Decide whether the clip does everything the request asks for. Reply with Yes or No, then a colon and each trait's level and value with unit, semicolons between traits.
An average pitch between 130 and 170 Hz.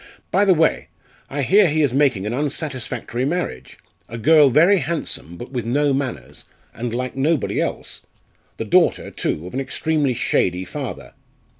Yes: low, 135 Hz